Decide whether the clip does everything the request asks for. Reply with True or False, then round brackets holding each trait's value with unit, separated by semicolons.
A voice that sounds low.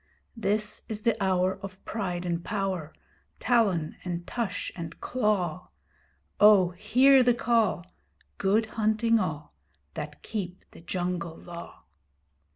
False (190 Hz)